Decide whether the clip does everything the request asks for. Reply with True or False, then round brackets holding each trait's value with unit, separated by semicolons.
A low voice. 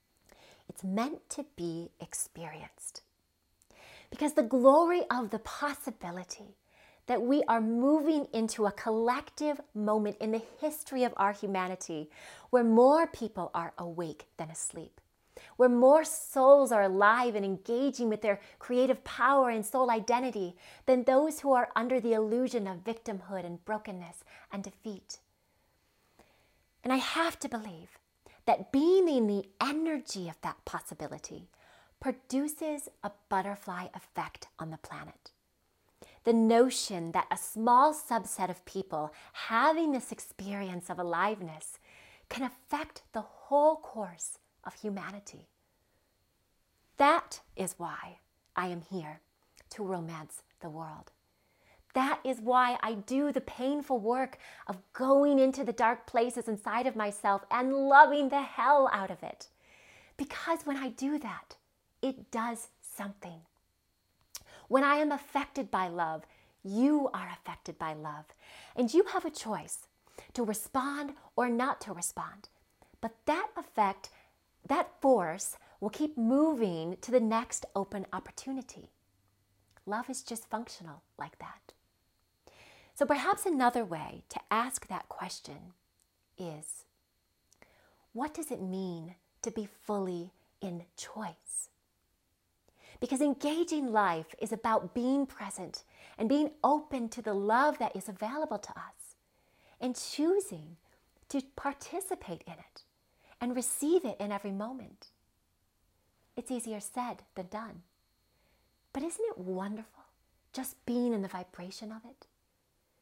False (230 Hz)